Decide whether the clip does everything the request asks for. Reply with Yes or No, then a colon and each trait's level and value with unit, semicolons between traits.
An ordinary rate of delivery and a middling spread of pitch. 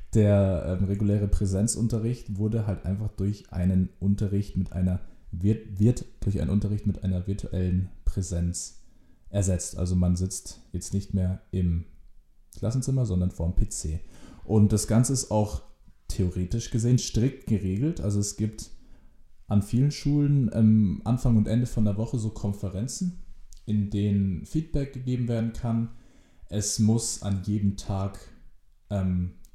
Yes: average, 140 wpm; average, 3.6 semitones